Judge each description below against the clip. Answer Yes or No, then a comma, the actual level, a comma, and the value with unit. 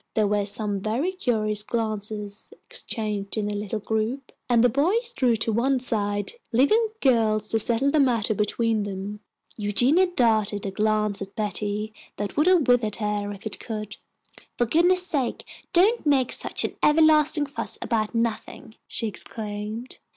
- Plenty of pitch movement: No, average, 4.4 semitones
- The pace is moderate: Yes, average, 160 wpm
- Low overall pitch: No, high, 220 Hz